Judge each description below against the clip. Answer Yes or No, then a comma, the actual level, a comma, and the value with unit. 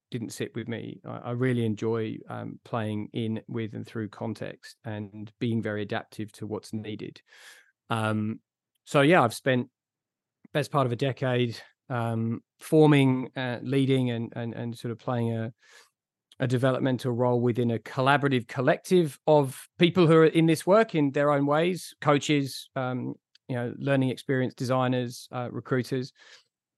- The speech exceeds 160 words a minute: No, average, 155 wpm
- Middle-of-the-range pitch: No, low, 125 Hz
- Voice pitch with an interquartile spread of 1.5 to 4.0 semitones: Yes, average, 3.3 semitones